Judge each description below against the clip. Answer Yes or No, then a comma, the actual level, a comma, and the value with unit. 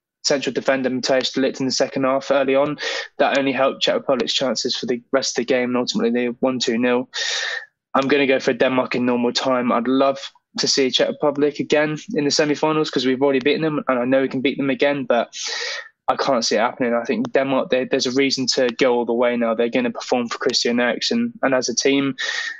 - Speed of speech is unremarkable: No, fast, 240 wpm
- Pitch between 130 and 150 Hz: Yes, low, 135 Hz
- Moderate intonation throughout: No, narrow, 2.3 semitones